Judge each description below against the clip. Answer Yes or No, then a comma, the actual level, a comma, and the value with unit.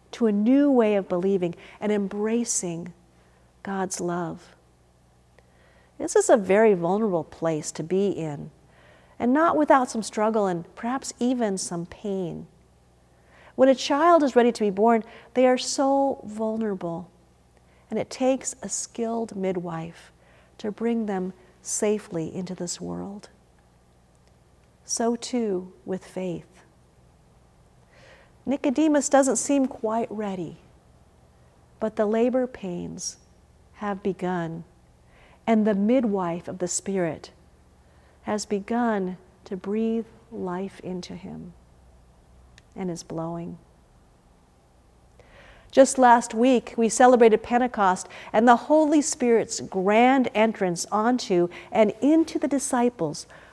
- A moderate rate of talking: No, slow, 115 wpm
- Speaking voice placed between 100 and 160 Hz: No, high, 190 Hz